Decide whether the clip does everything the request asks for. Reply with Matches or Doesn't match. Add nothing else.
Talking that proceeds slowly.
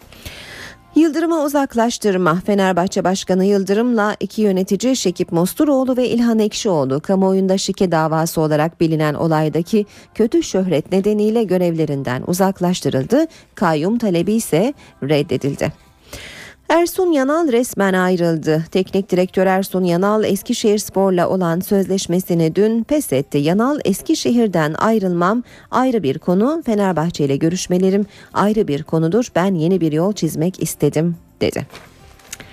Doesn't match